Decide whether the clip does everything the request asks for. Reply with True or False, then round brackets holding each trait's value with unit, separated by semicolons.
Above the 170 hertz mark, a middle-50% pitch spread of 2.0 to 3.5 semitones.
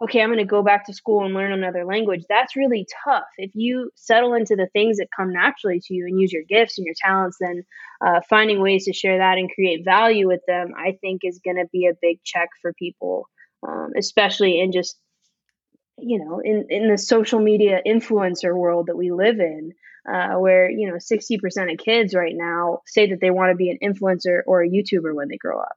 True (190 Hz; 3.0 semitones)